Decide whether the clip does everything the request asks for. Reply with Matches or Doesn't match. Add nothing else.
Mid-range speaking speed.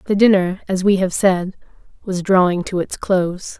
Matches